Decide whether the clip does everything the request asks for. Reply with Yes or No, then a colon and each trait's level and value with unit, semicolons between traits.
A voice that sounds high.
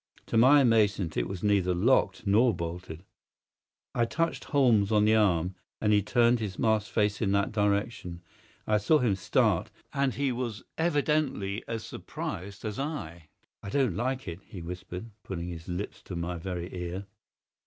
No: low, 105 Hz